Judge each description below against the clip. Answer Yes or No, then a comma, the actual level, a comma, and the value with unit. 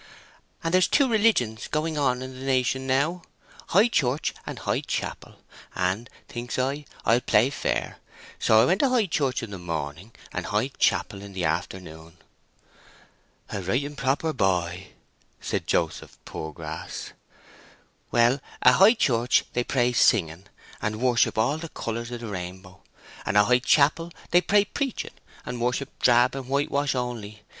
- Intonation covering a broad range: Yes, wide, 5.7 semitones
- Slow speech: No, average, 155 wpm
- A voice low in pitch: Yes, low, 125 Hz